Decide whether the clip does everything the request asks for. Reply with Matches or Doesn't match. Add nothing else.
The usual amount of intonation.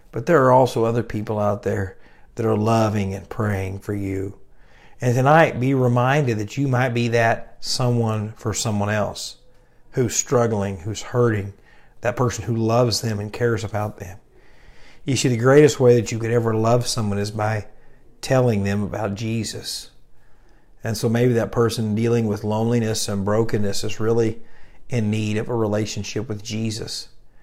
Doesn't match